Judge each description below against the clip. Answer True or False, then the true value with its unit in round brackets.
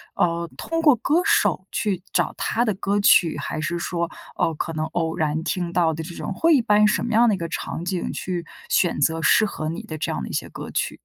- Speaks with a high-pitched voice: False (175 Hz)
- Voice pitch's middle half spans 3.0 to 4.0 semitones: False (4.6 semitones)